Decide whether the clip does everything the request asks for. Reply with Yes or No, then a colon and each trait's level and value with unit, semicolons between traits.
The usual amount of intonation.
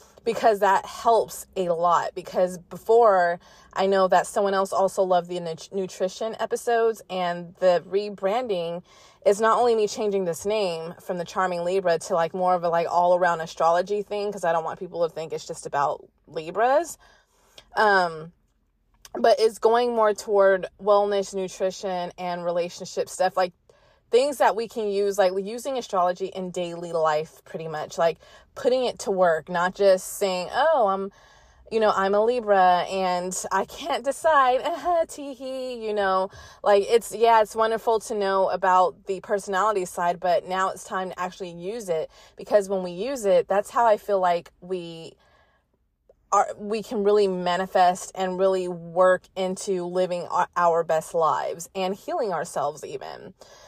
Yes: average, 3.1 semitones